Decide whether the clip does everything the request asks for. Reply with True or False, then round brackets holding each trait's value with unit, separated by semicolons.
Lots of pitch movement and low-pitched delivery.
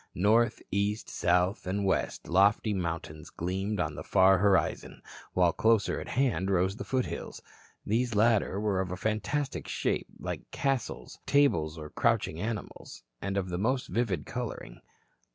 False (3.6 semitones; 100 Hz)